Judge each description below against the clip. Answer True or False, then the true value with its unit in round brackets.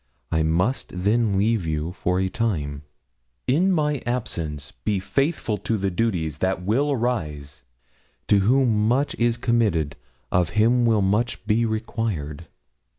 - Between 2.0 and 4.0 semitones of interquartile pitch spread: False (5.5 semitones)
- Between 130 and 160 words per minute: True (140 wpm)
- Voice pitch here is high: False (105 Hz)